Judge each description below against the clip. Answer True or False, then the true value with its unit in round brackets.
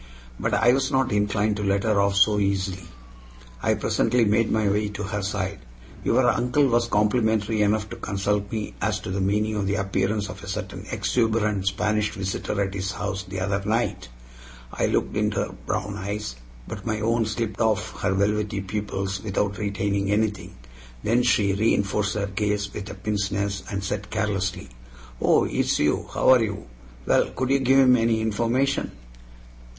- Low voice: True (105 Hz)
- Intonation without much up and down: True (1.9 semitones)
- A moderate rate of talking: True (175 wpm)